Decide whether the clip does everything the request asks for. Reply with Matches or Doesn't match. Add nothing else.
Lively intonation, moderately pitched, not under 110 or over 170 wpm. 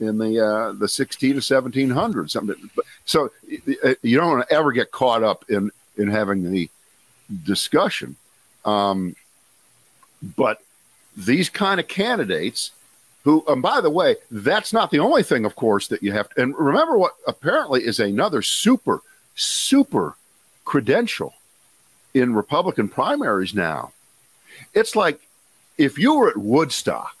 Doesn't match